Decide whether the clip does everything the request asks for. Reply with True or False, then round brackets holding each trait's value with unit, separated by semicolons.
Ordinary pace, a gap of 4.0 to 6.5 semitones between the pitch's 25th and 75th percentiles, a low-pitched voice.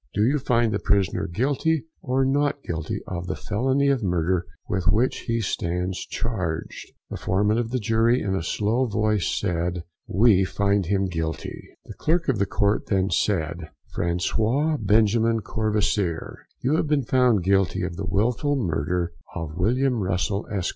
True (160 wpm; 5.2 semitones; 105 Hz)